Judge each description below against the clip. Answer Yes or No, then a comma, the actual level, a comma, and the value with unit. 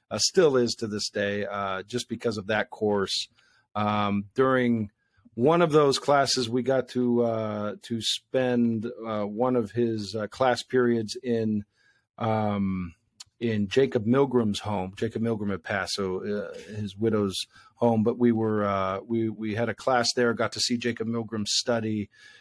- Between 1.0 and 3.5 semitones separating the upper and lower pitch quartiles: Yes, narrow, 2.6 semitones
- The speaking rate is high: No, average, 165 wpm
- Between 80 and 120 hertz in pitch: Yes, low, 115 Hz